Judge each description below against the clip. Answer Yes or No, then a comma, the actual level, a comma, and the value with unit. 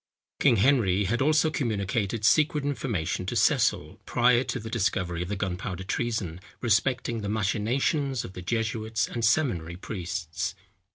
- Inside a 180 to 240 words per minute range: No, average, 145 wpm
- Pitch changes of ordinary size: Yes, average, 4.5 semitones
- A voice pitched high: No, low, 110 Hz